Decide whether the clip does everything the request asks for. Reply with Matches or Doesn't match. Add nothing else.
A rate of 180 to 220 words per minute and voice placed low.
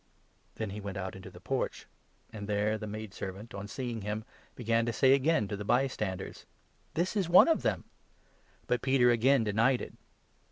Matches